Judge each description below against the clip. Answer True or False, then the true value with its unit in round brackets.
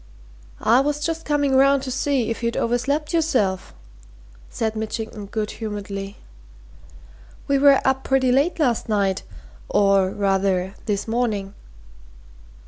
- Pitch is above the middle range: True (230 Hz)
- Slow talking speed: True (125 wpm)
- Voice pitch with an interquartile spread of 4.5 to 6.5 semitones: True (5.3 semitones)